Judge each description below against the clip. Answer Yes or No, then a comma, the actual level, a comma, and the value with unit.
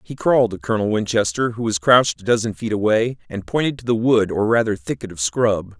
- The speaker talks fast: Yes, fast, 230 wpm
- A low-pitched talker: Yes, low, 110 Hz